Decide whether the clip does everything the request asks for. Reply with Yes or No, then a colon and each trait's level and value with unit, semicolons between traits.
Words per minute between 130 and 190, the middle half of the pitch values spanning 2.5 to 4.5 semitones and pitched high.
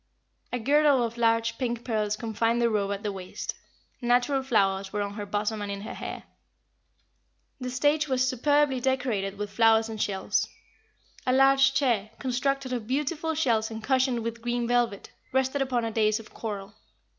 Yes: average, 170 wpm; average, 3.6 semitones; high, 235 Hz